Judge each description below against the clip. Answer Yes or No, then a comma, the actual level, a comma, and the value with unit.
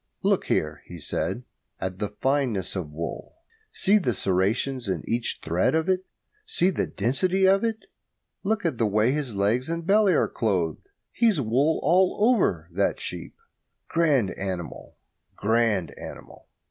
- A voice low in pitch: Yes, low, 125 Hz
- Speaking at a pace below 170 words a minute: Yes, average, 155 wpm